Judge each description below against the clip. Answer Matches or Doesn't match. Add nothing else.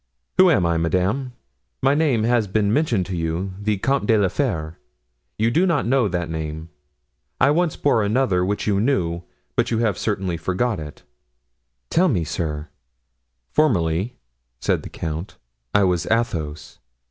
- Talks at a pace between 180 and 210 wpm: Doesn't match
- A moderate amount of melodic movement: Doesn't match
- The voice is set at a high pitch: Doesn't match